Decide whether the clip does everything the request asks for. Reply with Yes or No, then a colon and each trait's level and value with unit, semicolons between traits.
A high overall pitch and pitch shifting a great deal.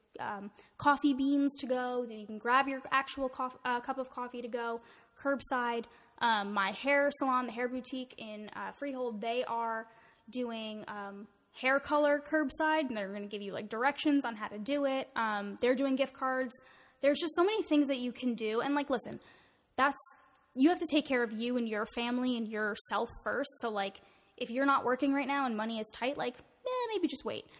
No: very high, 255 Hz; average, 3.3 semitones